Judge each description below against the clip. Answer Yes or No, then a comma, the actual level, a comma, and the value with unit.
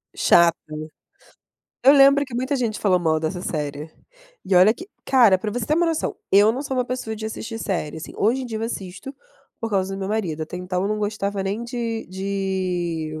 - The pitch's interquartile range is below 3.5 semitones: No, average, 4.7 semitones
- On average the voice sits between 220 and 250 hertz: No, high, 205 Hz